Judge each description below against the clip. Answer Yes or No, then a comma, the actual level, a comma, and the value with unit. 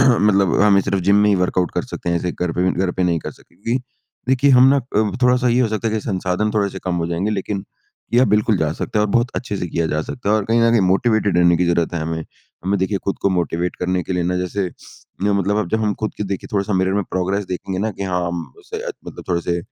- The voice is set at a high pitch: No, low, 100 Hz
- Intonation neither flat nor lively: Yes, average, 3.2 semitones